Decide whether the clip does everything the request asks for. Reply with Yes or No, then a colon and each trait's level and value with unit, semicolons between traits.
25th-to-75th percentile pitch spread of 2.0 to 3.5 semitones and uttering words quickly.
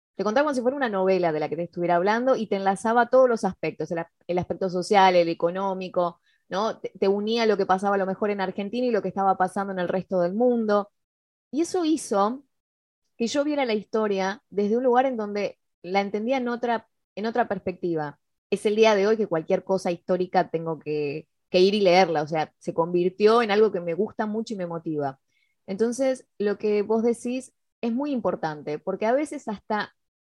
No: average, 4.0 semitones; fast, 215 wpm